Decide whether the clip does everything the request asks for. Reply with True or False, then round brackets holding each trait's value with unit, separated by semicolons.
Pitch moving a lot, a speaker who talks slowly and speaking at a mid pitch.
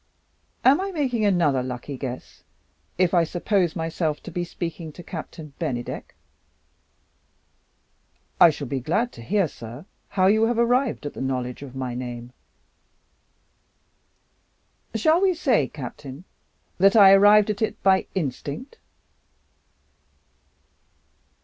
True (7.7 semitones; 125 wpm; 170 Hz)